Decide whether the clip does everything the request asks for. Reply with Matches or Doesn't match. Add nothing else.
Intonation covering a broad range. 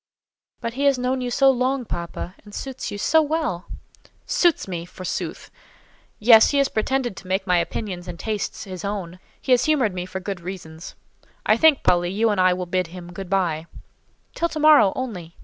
Matches